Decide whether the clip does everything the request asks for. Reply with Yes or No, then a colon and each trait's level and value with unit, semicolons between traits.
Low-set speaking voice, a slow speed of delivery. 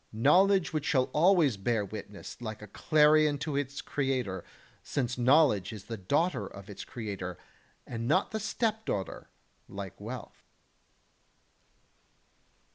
Yes: low, 130 Hz; slow, 120 wpm